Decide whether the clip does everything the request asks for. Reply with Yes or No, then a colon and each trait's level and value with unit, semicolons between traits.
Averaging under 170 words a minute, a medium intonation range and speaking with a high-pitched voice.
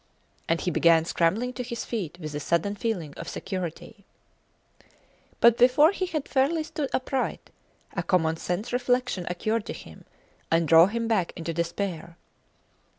No: average, 150 wpm; wide, 6.8 semitones; high, 200 Hz